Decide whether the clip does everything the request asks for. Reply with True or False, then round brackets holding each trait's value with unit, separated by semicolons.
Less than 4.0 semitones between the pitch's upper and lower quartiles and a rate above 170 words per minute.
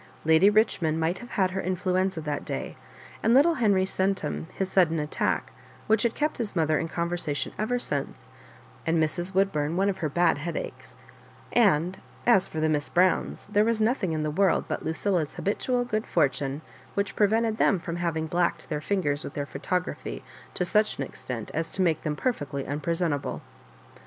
False (4.5 semitones; 180 wpm)